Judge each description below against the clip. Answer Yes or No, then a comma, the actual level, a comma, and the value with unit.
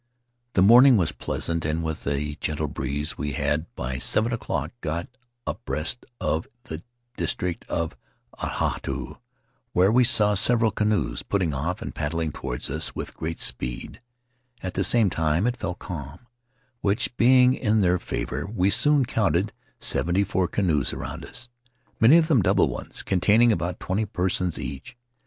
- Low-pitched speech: Yes, very low, 90 Hz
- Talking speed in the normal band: Yes, average, 155 wpm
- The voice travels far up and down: Yes, wide, 6.1 semitones